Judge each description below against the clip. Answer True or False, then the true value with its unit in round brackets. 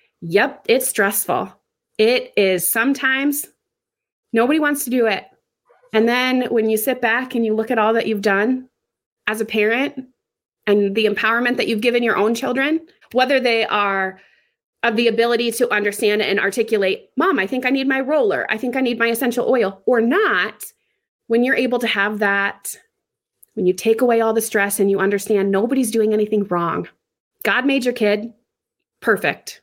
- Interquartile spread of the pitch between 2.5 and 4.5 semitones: True (3.4 semitones)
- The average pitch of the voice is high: True (230 Hz)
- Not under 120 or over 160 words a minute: False (180 wpm)